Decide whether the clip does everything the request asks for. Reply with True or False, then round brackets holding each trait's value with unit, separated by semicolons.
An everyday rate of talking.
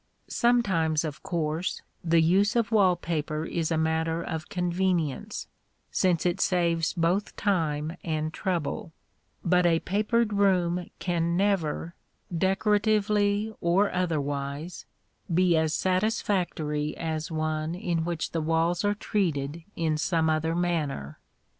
False (120 wpm)